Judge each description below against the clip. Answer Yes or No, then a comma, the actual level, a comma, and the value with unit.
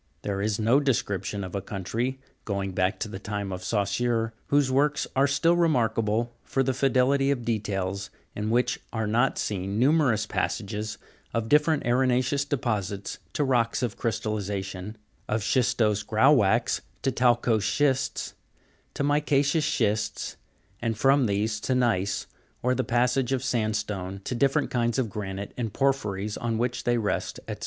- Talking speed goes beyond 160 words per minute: No, average, 150 wpm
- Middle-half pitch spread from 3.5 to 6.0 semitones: Yes, average, 4.1 semitones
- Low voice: Yes, low, 115 Hz